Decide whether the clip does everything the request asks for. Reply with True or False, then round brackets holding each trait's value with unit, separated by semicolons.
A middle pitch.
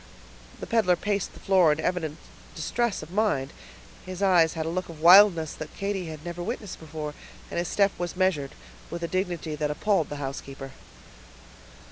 True (175 Hz)